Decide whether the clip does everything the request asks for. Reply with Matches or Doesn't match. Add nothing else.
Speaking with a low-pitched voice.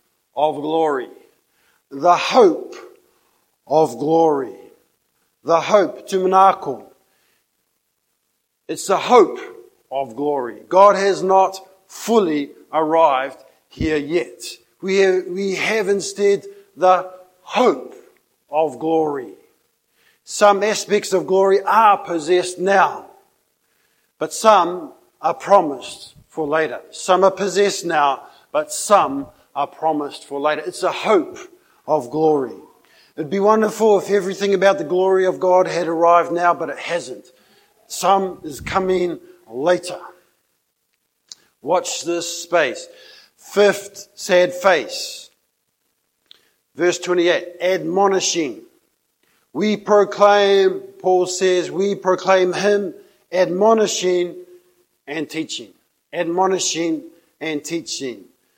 Doesn't match